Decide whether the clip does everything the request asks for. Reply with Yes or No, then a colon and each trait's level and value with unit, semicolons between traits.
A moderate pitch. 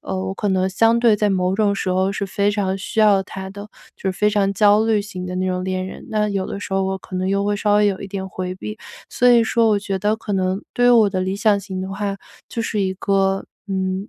No: high, 195 Hz